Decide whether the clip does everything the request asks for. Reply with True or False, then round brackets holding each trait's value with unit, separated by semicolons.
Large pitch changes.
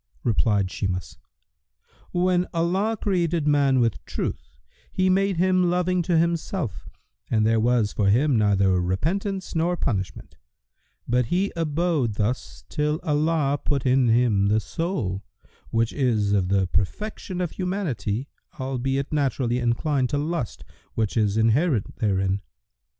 True (8.0 semitones)